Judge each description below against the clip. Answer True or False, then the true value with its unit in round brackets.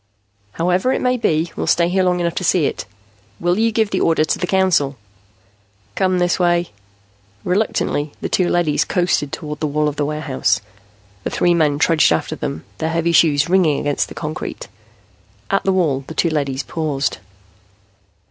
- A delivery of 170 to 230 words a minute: True (175 wpm)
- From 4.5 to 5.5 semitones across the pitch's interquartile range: False (3.2 semitones)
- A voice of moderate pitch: True (165 Hz)